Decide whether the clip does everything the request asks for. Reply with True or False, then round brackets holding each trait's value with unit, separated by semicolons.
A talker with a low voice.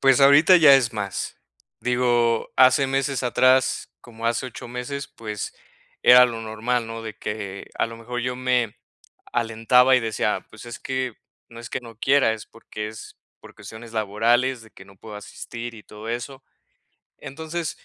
True (120 Hz)